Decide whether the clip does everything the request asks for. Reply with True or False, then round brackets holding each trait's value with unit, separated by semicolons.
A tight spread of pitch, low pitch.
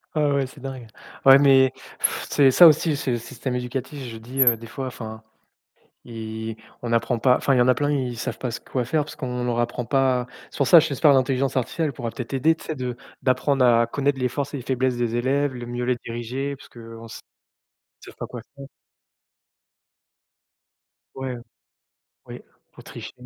True (2.3 semitones; 130 Hz)